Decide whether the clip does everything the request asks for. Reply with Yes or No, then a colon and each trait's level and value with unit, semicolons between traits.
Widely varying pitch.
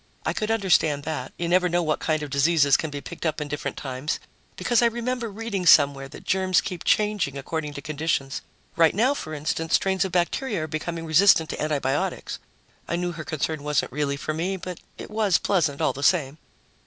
No: average, 4.2 semitones